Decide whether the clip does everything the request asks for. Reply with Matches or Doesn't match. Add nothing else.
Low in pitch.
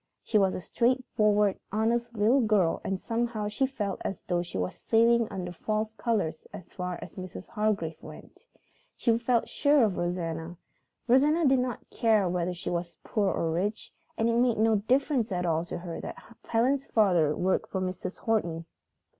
Doesn't match